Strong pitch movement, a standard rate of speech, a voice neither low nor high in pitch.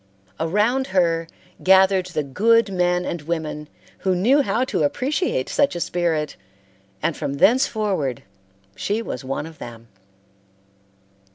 No: wide, 5.7 semitones; slow, 125 wpm; medium, 180 Hz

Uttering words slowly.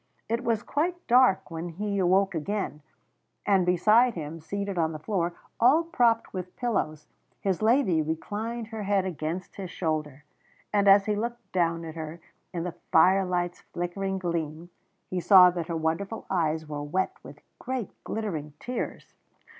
No: average, 155 wpm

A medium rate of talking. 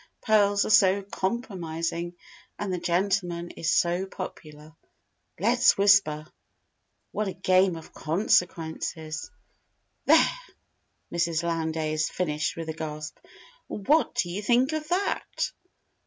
No: slow, 110 wpm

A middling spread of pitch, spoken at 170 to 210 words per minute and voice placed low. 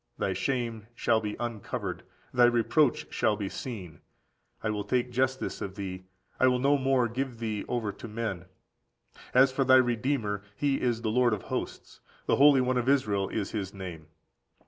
Yes: average, 3.8 semitones; average, 175 wpm; low, 120 Hz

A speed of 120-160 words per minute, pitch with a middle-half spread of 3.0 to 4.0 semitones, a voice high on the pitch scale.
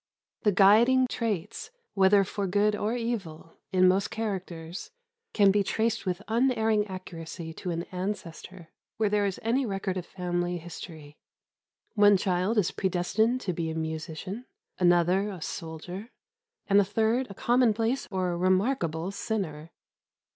Yes: average, 140 wpm; average, 3.7 semitones; high, 195 Hz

